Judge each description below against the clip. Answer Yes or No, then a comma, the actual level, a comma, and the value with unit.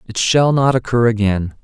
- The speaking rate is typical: Yes, average, 185 wpm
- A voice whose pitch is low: Yes, low, 115 Hz